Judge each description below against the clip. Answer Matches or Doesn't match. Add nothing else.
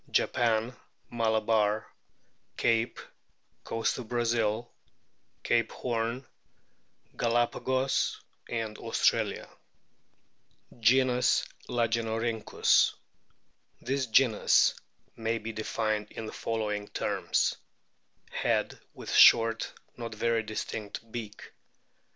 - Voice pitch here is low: Matches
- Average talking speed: Doesn't match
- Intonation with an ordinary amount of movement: Doesn't match